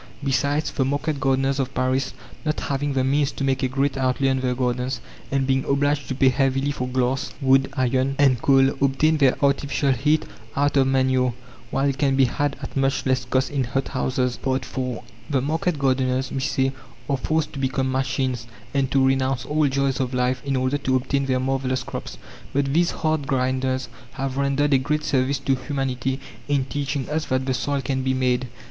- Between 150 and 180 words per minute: No, average, 195 wpm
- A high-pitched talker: No, low, 135 Hz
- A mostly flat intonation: Yes, narrow, 1.2 semitones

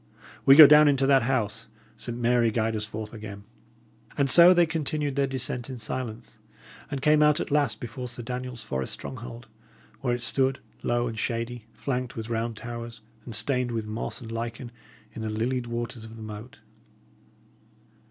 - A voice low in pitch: Yes, low, 120 Hz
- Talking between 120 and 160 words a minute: No, average, 175 wpm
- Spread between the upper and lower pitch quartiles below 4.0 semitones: Yes, average, 2.9 semitones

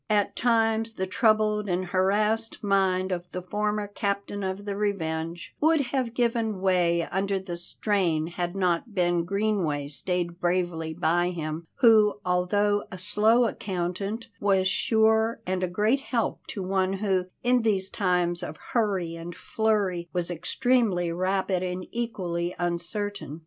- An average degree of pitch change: Yes, average, 3.3 semitones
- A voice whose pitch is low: No, high, 190 Hz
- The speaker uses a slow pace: No, average, 145 wpm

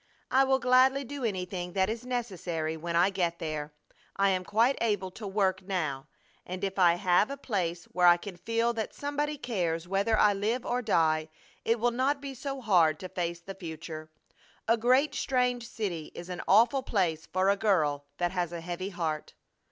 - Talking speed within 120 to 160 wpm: No, average, 190 wpm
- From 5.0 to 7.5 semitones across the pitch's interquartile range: Yes, wide, 5.4 semitones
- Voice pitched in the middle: No, high, 195 Hz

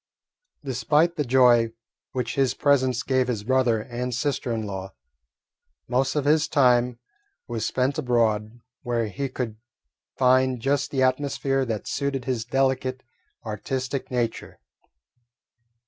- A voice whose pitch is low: Yes, low, 130 Hz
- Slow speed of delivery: Yes, slow, 125 wpm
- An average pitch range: No, narrow, 2.3 semitones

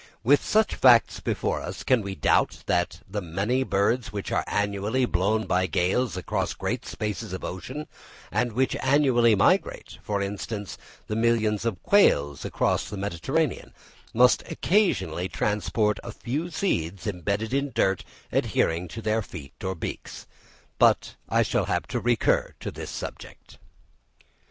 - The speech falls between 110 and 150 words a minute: Yes, average, 140 wpm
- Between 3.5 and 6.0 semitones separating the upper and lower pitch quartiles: Yes, average, 4.6 semitones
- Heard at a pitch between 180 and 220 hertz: No, low, 105 Hz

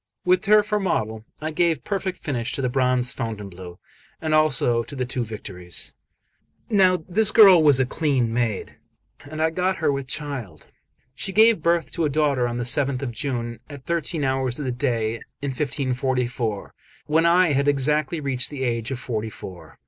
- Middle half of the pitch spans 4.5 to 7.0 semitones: Yes, average, 4.9 semitones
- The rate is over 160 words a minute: Yes, average, 180 wpm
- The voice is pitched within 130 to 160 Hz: Yes, low, 135 Hz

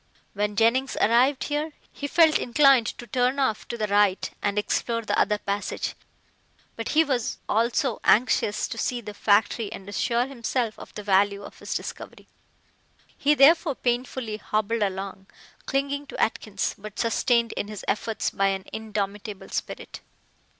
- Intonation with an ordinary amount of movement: Yes, average, 3.9 semitones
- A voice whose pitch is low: No, high, 225 Hz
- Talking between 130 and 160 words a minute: Yes, average, 155 wpm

